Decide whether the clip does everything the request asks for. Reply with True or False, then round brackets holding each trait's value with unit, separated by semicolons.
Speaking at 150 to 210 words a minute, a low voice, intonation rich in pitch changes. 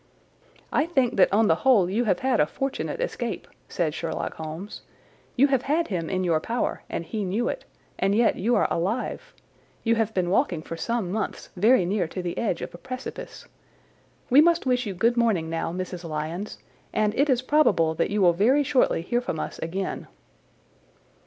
False (190 wpm; 210 Hz; 6.1 semitones)